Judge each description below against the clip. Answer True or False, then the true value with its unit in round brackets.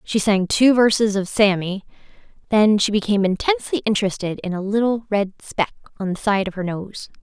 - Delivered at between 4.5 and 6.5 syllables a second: True (5.5 syllables/s)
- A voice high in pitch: True (205 Hz)